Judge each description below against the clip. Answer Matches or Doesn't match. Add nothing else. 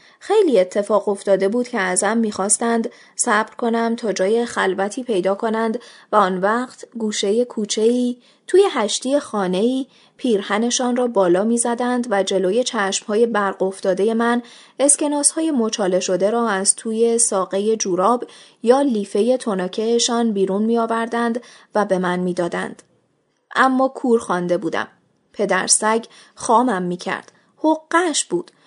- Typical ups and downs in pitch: Matches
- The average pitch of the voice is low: Doesn't match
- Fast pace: Doesn't match